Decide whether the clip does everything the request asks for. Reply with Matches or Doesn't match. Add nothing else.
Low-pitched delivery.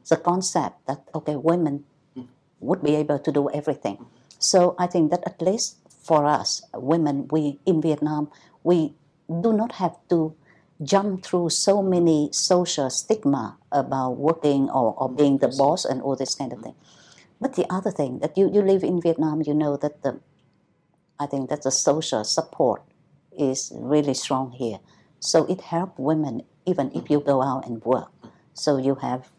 Doesn't match